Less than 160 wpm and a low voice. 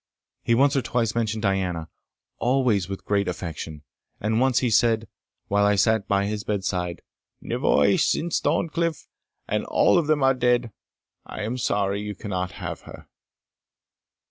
Yes: average, 150 wpm; low, 105 Hz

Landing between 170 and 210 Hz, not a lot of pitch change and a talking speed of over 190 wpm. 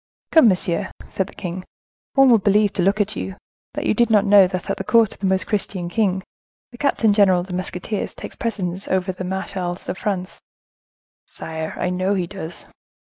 Yes: high, 190 Hz; narrow, 2.3 semitones; average, 200 wpm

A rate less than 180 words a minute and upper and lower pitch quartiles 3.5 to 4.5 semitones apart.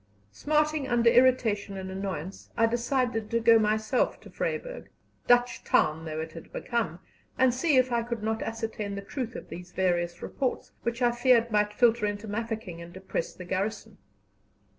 Yes: average, 170 wpm; average, 3.9 semitones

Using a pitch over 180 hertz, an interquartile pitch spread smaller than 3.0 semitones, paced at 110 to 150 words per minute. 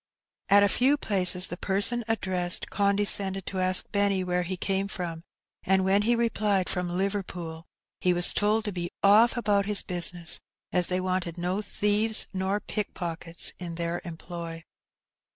No: high, 190 Hz; narrow, 2.5 semitones; average, 165 wpm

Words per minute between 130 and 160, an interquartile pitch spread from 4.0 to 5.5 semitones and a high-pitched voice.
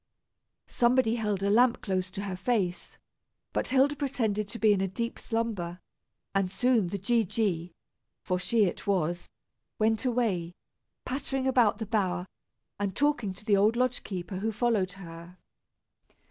Yes: average, 155 wpm; average, 4.3 semitones; high, 210 Hz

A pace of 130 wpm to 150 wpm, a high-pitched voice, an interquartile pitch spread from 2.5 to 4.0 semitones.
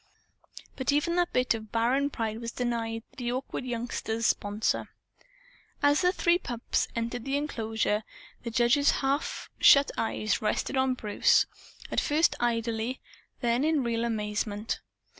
Yes: average, 140 wpm; high, 240 Hz; average, 3.4 semitones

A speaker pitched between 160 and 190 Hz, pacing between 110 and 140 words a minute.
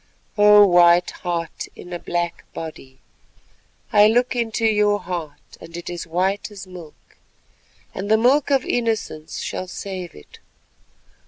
Yes: medium, 185 Hz; slow, 135 wpm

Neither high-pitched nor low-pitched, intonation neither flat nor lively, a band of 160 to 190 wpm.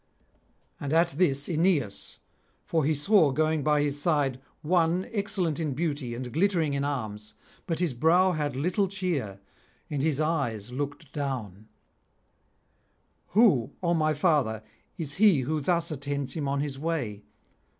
No: medium, 150 Hz; average, 3.6 semitones; average, 145 wpm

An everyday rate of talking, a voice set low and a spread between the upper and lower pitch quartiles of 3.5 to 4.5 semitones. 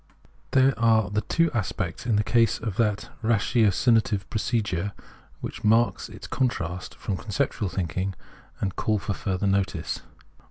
No: average, 150 wpm; low, 105 Hz; average, 3.0 semitones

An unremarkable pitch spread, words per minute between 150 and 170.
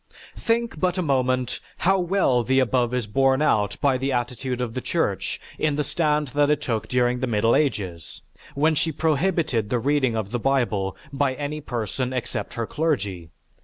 No: average, 4.2 semitones; average, 180 wpm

